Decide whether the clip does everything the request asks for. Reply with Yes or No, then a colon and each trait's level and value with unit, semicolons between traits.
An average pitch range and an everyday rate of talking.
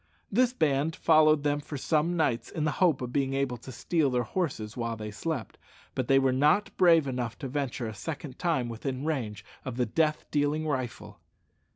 Yes: average, 4.1 semitones; average, 195 wpm